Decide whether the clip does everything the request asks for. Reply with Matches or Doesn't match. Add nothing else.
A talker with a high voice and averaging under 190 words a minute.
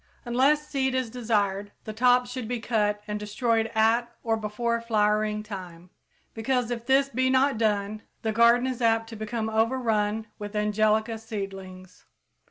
Matches